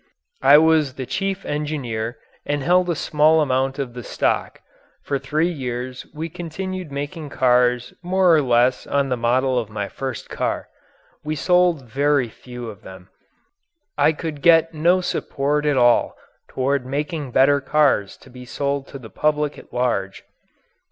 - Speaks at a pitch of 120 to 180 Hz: Yes, medium, 140 Hz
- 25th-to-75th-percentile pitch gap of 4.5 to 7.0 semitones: No, average, 3.8 semitones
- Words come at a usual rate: Yes, average, 160 wpm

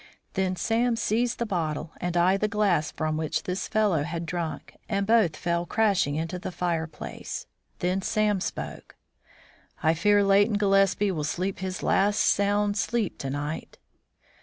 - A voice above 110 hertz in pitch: Yes, high, 190 Hz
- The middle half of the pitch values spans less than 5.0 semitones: Yes, average, 3.8 semitones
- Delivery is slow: No, average, 155 wpm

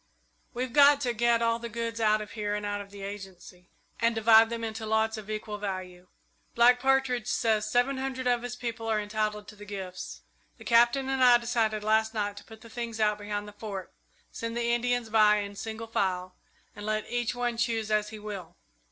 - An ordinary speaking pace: No, fast, 210 wpm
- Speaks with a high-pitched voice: Yes, high, 220 Hz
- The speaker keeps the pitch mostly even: Yes, narrow, 2.3 semitones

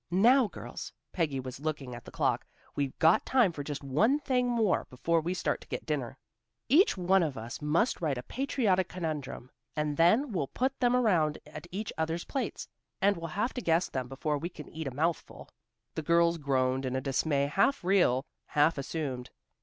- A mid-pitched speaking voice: Yes, medium, 160 Hz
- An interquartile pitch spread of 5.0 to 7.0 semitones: Yes, wide, 5.6 semitones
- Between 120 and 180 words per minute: No, average, 195 wpm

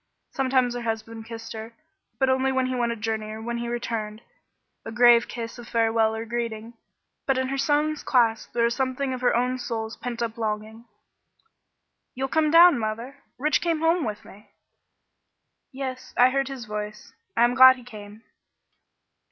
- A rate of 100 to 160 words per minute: No, average, 175 wpm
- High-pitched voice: Yes, high, 235 Hz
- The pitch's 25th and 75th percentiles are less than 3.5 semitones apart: Yes, average, 2.7 semitones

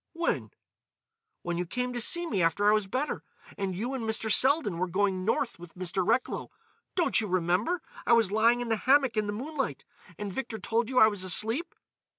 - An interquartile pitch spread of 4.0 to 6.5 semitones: Yes, average, 5.2 semitones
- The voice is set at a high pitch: Yes, high, 220 Hz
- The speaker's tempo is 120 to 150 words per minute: No, average, 200 wpm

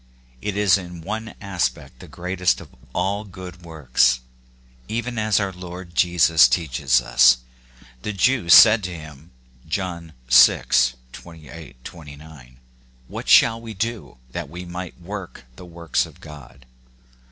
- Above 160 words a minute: No, average, 140 wpm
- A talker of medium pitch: No, very low, 85 Hz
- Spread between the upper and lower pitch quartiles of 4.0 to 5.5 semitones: Yes, average, 4.8 semitones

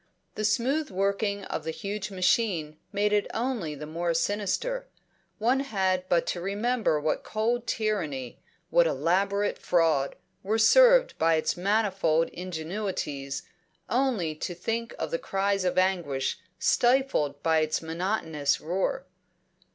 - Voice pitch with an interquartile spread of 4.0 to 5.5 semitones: Yes, average, 5.2 semitones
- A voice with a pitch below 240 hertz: Yes, high, 190 Hz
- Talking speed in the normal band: No, slow, 130 wpm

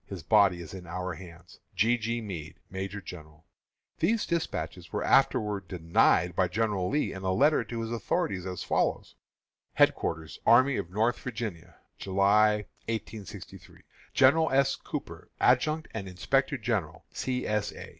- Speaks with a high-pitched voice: No, low, 100 Hz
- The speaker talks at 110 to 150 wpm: Yes, average, 145 wpm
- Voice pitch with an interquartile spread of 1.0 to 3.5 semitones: No, average, 4.6 semitones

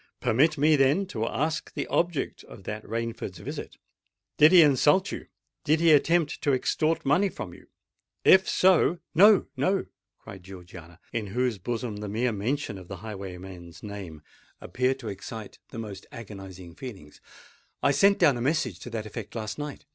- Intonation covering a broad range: Yes, wide, 7.2 semitones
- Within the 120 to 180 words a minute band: Yes, average, 165 wpm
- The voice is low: Yes, low, 115 Hz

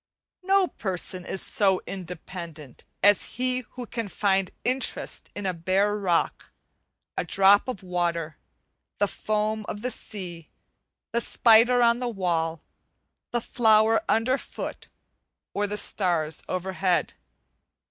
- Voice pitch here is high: Yes, high, 200 Hz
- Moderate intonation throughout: Yes, average, 4.1 semitones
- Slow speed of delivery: Yes, slow, 120 wpm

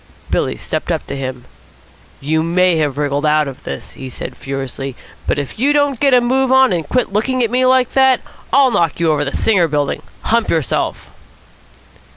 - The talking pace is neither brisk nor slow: Yes, average, 190 wpm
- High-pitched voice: No, medium, 170 Hz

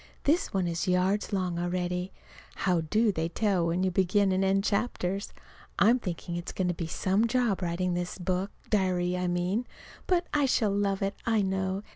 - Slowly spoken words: No, average, 185 wpm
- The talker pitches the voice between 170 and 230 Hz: Yes, high, 190 Hz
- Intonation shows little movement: Yes, narrow, 2.3 semitones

